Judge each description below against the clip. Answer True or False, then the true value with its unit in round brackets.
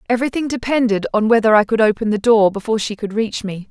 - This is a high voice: True (220 Hz)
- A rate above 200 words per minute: True (225 wpm)